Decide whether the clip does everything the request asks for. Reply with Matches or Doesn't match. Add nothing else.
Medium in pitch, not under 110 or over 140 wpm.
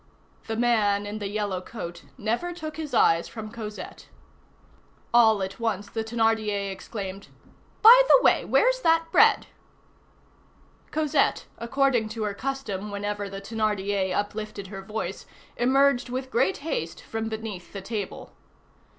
Doesn't match